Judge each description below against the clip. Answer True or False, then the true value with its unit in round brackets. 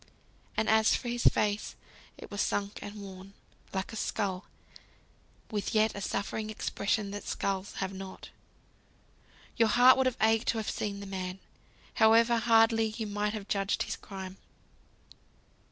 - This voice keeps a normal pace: True (155 wpm)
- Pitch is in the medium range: False (210 Hz)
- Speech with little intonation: True (2.1 semitones)